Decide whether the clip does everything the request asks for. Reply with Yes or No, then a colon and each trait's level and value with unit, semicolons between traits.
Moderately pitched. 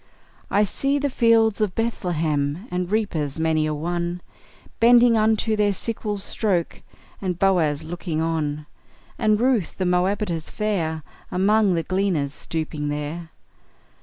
Yes: medium, 180 Hz